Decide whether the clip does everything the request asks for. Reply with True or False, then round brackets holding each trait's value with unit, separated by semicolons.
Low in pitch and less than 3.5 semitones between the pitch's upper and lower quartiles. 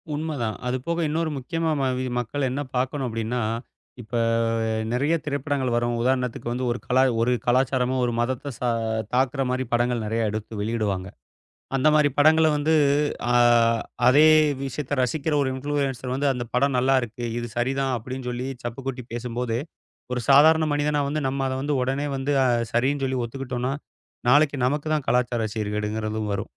True (130 Hz; 2.9 semitones)